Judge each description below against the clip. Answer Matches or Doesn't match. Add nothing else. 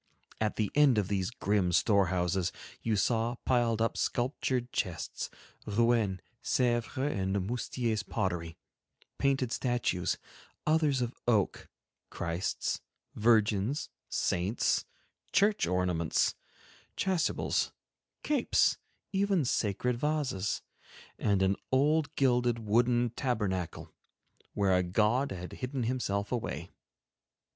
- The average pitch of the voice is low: Matches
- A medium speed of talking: Doesn't match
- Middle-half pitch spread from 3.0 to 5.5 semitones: Matches